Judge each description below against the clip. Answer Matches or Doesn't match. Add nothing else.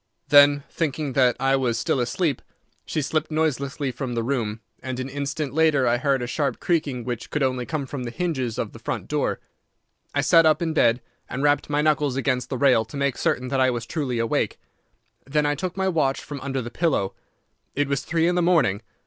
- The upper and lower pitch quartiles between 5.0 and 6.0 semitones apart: Doesn't match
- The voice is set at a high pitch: Doesn't match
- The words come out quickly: Matches